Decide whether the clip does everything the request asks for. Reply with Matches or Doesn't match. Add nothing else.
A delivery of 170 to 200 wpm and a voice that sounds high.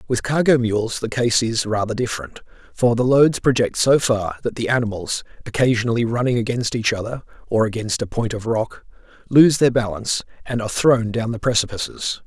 Doesn't match